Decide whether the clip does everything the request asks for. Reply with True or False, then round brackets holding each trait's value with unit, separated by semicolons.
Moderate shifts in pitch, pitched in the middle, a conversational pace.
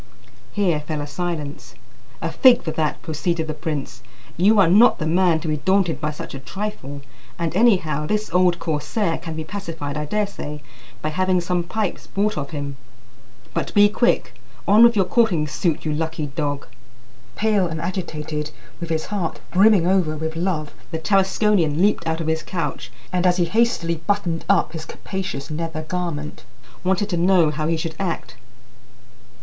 True (3.7 semitones; 165 Hz; 175 wpm)